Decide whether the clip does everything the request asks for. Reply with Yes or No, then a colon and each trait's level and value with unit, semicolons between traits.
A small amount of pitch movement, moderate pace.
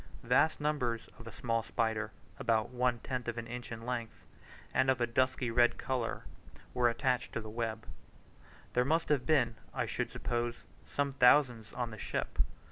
Yes: narrow, 1.9 semitones; average, 175 wpm